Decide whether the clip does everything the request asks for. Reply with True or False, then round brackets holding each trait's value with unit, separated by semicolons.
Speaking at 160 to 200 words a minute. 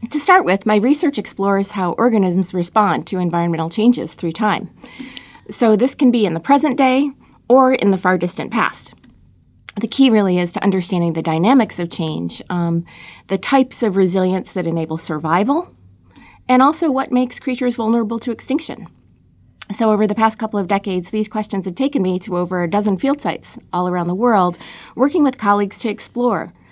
True (180 wpm)